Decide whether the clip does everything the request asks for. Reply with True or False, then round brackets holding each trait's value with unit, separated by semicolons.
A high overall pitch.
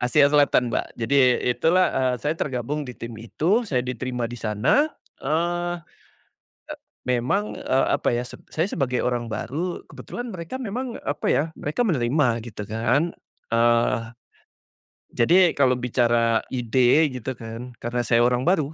False (130 Hz)